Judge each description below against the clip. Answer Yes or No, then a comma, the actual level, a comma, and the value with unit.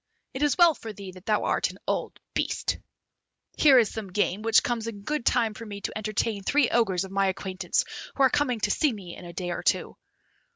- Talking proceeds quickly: Yes, fast, 225 wpm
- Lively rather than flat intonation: No, average, 4.0 semitones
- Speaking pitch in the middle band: No, high, 215 Hz